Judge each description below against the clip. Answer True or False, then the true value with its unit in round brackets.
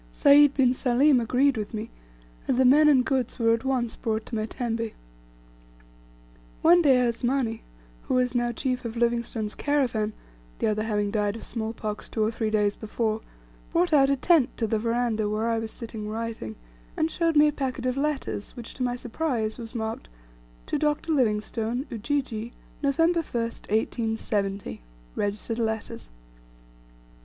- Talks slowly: False (165 wpm)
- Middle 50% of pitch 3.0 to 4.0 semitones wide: True (3.4 semitones)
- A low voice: False (235 Hz)